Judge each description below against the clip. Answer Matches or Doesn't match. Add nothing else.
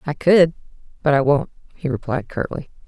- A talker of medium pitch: Matches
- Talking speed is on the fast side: Doesn't match